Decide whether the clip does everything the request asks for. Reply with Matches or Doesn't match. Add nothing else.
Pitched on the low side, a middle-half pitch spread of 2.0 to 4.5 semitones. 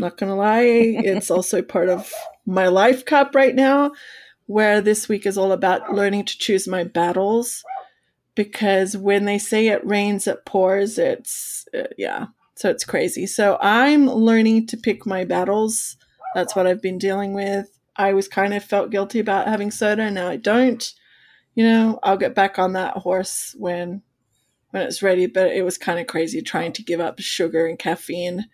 Doesn't match